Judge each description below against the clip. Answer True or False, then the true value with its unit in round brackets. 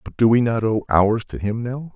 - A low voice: True (115 Hz)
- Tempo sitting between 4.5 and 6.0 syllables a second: True (5.1 syllables/s)